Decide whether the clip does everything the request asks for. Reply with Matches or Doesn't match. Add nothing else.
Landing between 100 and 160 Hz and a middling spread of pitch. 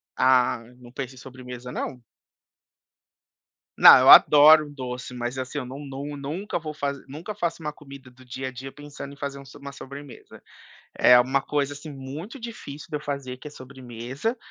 Doesn't match